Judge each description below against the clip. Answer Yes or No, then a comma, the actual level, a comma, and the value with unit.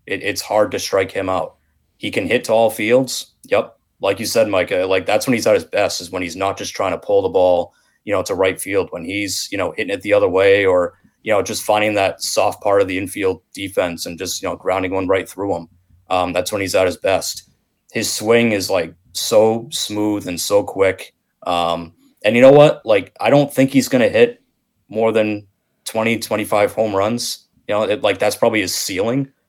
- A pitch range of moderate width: No, wide, 8.8 semitones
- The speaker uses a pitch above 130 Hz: No, low, 110 Hz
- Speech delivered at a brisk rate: Yes, fast, 230 wpm